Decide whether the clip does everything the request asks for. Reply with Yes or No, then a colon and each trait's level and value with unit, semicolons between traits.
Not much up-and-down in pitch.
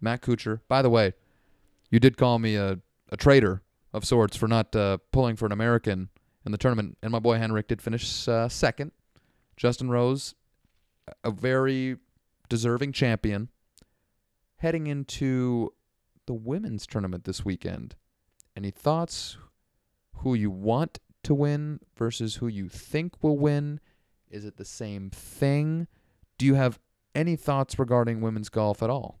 No: average, 4.4 semitones